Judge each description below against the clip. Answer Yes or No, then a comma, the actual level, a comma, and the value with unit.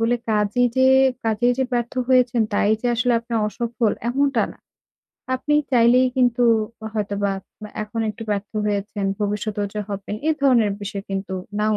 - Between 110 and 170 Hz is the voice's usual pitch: No, high, 225 Hz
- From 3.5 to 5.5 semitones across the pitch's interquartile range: No, average, 3.0 semitones